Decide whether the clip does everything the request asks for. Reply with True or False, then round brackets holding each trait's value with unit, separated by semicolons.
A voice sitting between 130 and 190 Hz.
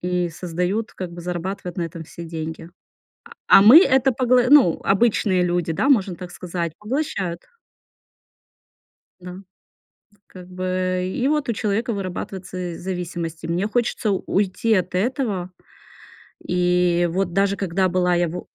True (185 Hz)